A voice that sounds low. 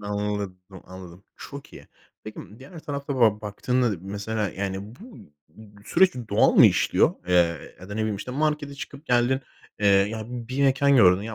Yes: low, 110 Hz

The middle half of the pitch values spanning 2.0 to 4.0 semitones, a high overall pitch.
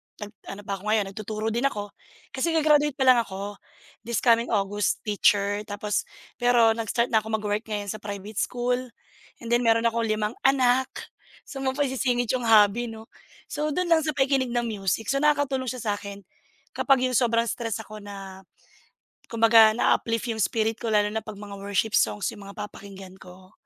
Yes: average, 3.2 semitones; high, 225 Hz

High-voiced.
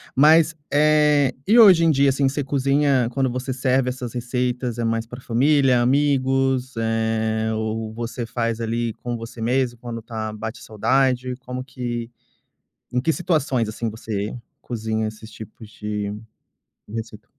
No: low, 125 Hz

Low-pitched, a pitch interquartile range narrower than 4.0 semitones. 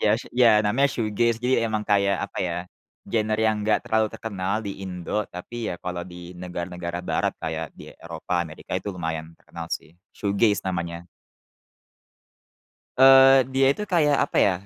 No: low, 100 Hz; average, 4.7 semitones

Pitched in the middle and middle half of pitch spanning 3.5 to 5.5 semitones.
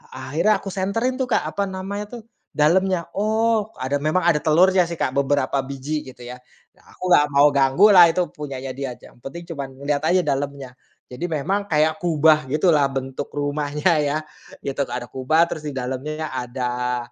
Yes: medium, 150 Hz; average, 5.0 semitones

